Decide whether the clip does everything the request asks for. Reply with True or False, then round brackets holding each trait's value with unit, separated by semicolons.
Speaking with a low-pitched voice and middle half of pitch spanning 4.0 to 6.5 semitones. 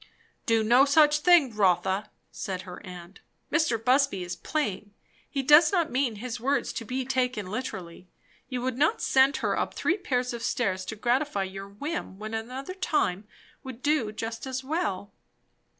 False (245 Hz; 5.5 semitones)